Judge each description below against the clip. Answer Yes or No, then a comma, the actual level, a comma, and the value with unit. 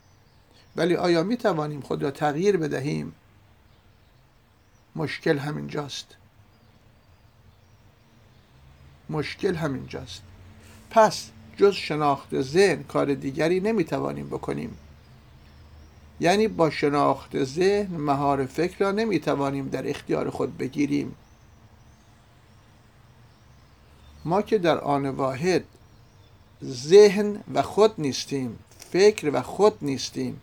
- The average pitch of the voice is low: Yes, low, 120 Hz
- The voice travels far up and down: Yes, wide, 6.3 semitones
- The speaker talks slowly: Yes, slow, 95 wpm